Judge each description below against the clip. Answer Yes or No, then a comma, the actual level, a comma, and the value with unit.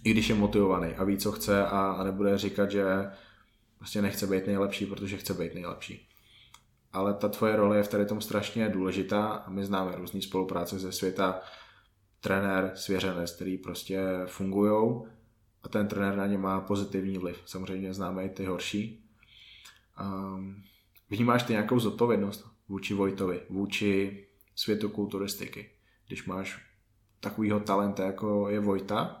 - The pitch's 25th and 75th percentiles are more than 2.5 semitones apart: No, narrow, 1.6 semitones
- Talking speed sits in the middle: Yes, average, 145 wpm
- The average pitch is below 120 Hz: Yes, low, 100 Hz